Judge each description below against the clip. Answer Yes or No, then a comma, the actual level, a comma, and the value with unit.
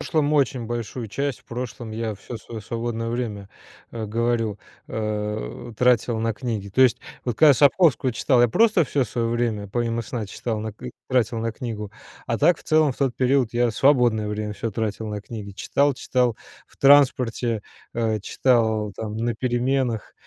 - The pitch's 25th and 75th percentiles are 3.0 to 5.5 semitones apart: No, narrow, 2.6 semitones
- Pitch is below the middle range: Yes, low, 115 Hz